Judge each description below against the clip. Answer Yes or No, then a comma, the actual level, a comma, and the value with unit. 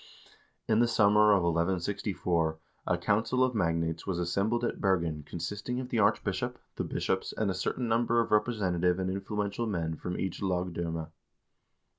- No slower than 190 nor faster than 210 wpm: No, average, 160 wpm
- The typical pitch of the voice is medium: No, very low, 95 Hz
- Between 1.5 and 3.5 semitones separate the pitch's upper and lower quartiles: No, average, 4.2 semitones